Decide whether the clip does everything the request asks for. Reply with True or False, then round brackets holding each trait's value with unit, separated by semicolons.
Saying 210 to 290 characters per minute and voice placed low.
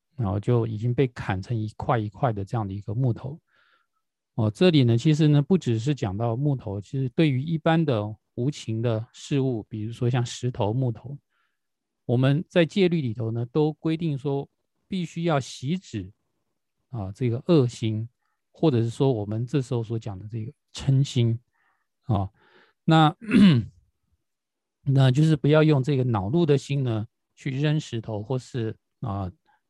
True (230 characters per minute; 125 Hz)